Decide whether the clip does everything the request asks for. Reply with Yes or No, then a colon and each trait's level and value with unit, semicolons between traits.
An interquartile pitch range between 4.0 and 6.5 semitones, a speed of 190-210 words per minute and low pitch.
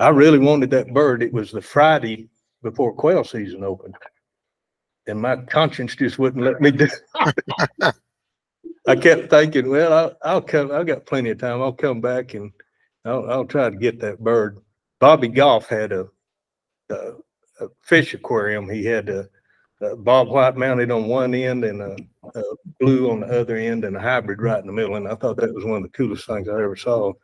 Yes: average, 4.6 semitones; average, 200 wpm; low, 125 Hz